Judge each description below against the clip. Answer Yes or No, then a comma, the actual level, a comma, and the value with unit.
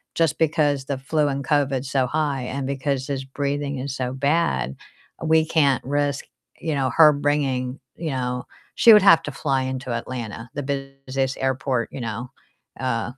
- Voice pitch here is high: No, low, 135 Hz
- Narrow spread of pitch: Yes, narrow, 2.0 semitones